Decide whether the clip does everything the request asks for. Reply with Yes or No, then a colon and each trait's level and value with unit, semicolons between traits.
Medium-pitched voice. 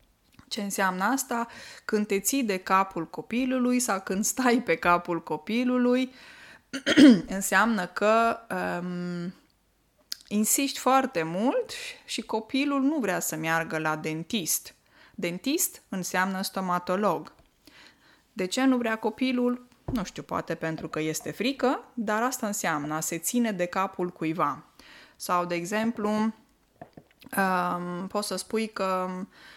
No: high, 205 Hz